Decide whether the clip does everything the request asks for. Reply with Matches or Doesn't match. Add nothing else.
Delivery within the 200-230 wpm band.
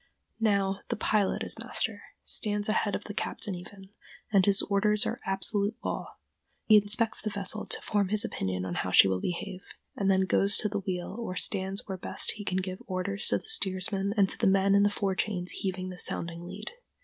Matches